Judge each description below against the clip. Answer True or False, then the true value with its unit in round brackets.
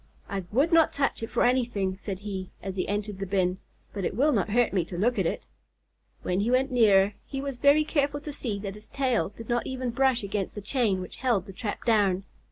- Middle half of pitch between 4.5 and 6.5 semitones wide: True (4.9 semitones)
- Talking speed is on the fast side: True (235 wpm)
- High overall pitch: True (215 Hz)